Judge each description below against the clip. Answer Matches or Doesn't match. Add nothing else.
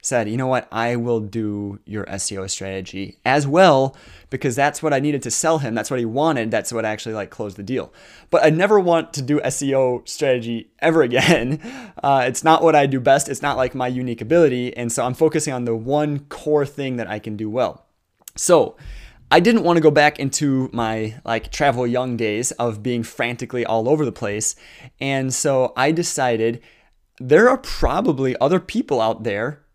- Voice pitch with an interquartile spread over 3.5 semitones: Matches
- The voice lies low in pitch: Matches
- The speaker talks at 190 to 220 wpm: Matches